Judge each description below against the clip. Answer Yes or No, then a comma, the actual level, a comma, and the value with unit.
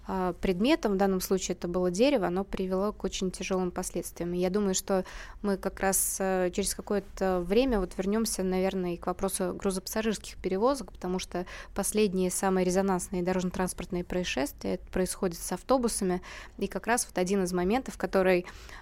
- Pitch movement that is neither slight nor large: No, narrow, 1.6 semitones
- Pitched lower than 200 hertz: Yes, high, 190 Hz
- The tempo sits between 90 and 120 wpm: No, average, 155 wpm